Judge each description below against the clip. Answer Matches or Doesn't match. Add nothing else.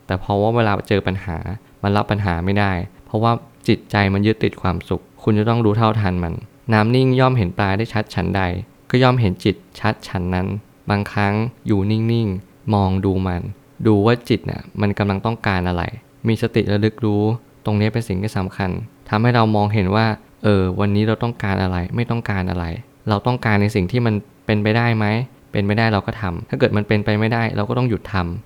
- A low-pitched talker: Matches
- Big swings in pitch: Doesn't match